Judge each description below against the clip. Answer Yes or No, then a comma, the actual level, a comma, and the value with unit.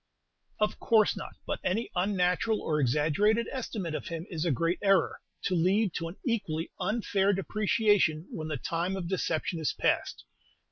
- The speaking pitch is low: No, medium, 180 Hz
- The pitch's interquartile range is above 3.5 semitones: Yes, average, 4.3 semitones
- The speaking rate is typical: Yes, average, 160 wpm